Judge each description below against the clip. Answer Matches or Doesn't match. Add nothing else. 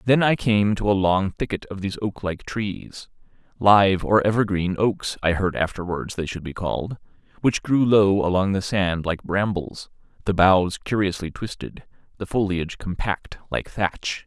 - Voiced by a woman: Doesn't match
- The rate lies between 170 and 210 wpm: Doesn't match